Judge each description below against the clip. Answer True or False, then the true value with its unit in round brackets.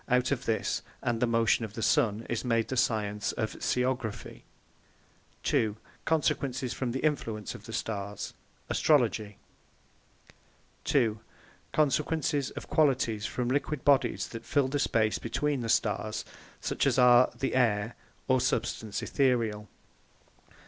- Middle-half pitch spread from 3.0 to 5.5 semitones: True (3.3 semitones)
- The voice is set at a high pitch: False (120 Hz)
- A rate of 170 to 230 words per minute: False (135 wpm)